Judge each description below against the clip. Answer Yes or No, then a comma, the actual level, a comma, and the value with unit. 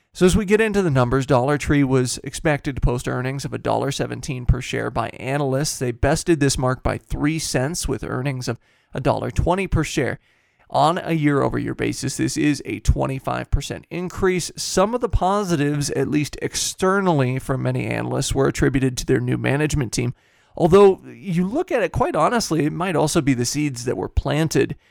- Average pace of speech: Yes, average, 185 wpm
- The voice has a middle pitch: Yes, medium, 145 Hz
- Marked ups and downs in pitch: No, average, 4.5 semitones